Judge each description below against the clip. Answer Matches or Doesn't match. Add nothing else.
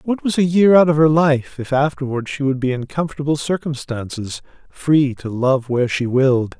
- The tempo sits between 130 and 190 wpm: Doesn't match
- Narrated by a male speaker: Matches